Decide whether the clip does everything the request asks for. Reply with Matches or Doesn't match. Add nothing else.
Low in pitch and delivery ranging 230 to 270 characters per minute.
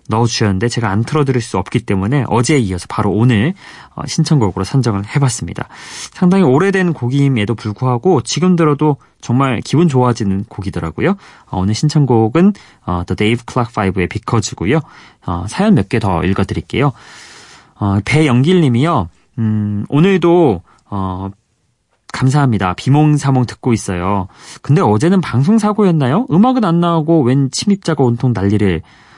Doesn't match